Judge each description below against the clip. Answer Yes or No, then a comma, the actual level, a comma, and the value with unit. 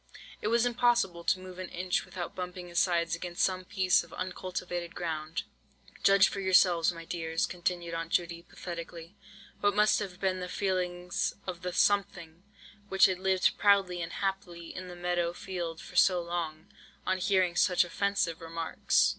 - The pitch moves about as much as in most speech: No, narrow, 1.7 semitones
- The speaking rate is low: No, average, 165 wpm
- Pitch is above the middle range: No, medium, 180 Hz